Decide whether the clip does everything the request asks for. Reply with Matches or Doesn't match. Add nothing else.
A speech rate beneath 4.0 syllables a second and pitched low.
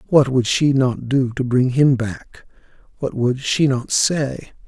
Matches